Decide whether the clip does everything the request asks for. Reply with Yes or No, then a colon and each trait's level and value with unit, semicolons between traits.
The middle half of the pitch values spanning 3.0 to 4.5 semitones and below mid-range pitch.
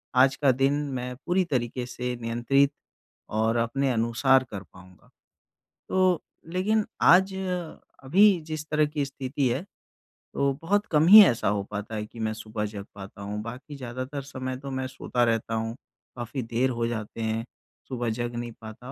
Yes: average, 3.6 semitones; low, 125 Hz